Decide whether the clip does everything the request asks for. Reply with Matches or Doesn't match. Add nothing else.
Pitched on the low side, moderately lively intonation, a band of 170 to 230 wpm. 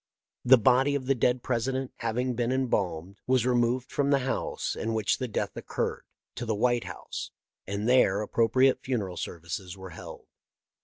Matches